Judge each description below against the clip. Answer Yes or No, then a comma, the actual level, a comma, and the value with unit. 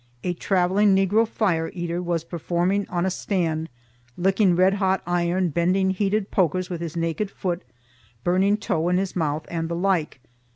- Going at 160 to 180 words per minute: Yes, average, 165 wpm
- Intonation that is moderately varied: No, narrow, 2.2 semitones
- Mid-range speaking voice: Yes, medium, 180 Hz